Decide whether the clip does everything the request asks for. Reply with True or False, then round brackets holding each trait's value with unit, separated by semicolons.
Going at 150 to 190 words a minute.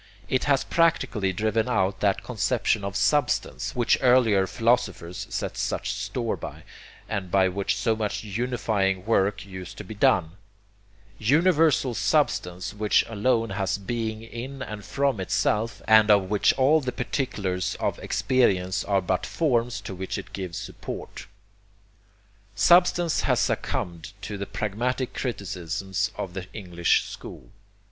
False (140 wpm)